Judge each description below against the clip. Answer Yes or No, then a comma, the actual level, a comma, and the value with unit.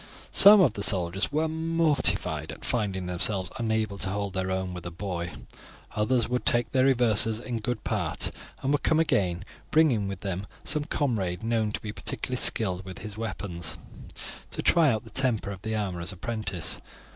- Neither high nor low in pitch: No, low, 105 Hz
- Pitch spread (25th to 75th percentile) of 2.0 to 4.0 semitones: No, average, 4.7 semitones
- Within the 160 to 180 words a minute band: Yes, average, 175 wpm